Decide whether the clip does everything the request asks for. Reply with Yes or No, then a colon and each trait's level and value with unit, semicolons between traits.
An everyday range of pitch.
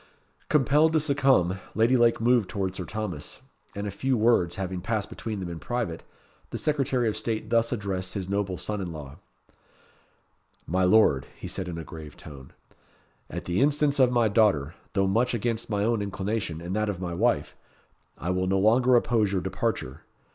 Yes: average, 4.4 semitones